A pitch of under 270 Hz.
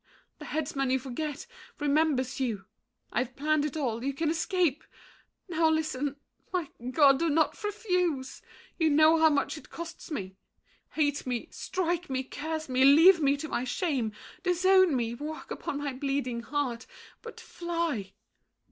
No: very high, 295 Hz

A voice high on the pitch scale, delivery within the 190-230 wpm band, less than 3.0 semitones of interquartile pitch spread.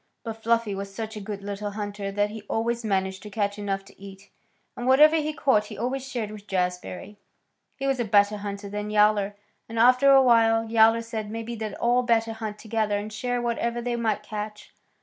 Yes: high, 215 Hz; fast, 205 wpm; narrow, 2.4 semitones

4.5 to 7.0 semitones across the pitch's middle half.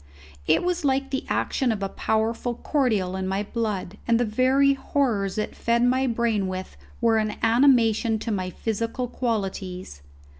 No: average, 4.0 semitones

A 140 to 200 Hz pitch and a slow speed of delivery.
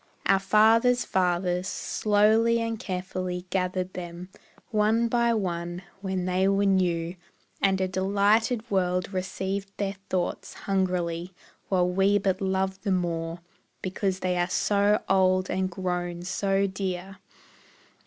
Yes: high, 190 Hz; slow, 125 wpm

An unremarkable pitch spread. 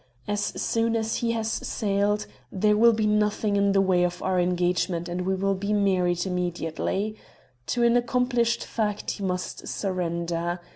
Yes: average, 3.1 semitones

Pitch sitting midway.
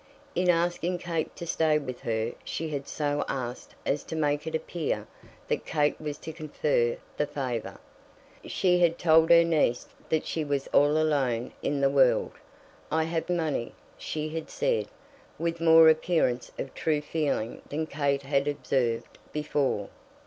Yes: medium, 150 Hz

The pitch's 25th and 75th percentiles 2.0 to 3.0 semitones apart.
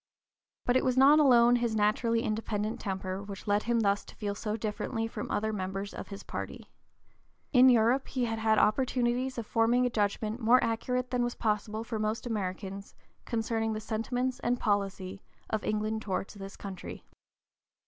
Yes: average, 2.7 semitones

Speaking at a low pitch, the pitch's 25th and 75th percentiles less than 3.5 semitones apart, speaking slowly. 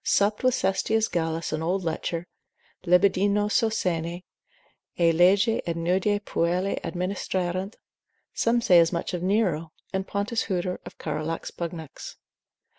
No: medium, 180 Hz; average, 3.1 semitones; slow, 125 wpm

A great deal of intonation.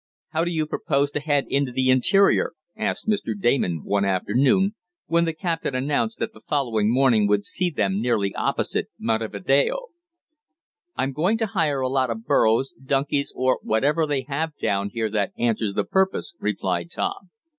Yes: wide, 6.3 semitones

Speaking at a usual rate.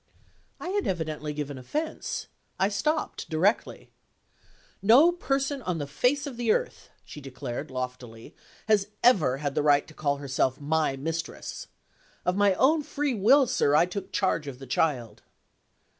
Yes: average, 155 wpm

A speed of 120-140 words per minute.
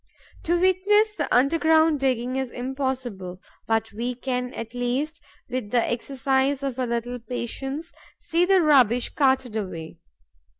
Yes: slow, 135 wpm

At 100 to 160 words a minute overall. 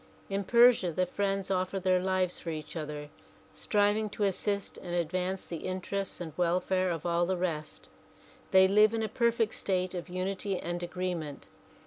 No: average, 170 wpm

